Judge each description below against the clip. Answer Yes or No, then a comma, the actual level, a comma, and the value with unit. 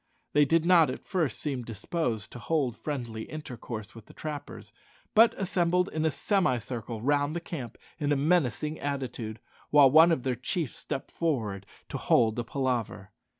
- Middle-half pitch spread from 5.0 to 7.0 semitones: Yes, average, 5.3 semitones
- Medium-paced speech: Yes, average, 165 wpm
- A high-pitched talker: No, medium, 140 Hz